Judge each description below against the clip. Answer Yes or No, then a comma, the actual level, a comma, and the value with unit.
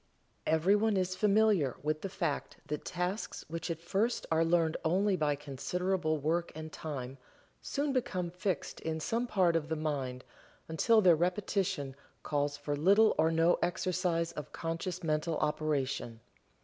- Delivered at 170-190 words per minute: No, average, 150 wpm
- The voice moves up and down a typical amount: Yes, average, 3.5 semitones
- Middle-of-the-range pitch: Yes, medium, 165 Hz